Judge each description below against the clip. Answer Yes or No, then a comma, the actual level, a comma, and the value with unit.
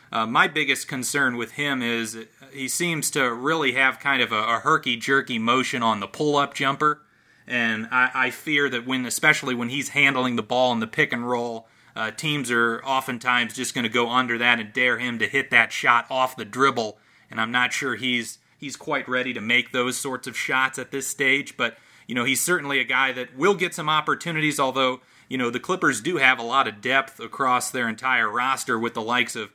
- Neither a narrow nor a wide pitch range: No, narrow, 2.3 semitones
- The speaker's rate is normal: No, fast, 220 wpm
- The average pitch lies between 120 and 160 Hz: Yes, low, 130 Hz